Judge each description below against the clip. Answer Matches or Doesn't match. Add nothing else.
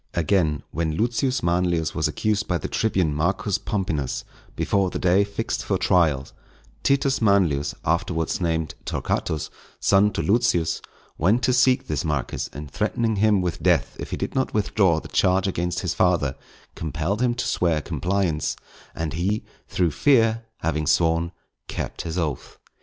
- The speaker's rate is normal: Matches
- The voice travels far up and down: Doesn't match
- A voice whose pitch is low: Matches